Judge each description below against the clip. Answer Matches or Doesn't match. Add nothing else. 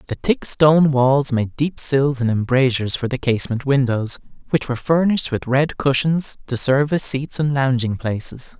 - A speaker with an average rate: Matches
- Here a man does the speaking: Matches